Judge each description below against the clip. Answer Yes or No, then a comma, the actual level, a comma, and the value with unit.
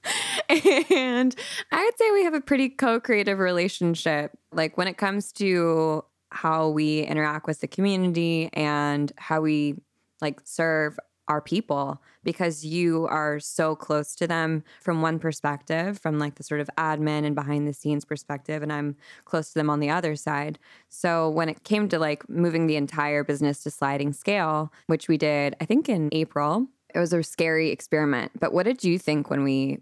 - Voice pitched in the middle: Yes, medium, 160 Hz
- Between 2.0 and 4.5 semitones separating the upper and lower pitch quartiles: Yes, average, 2.8 semitones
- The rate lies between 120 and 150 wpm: No, average, 185 wpm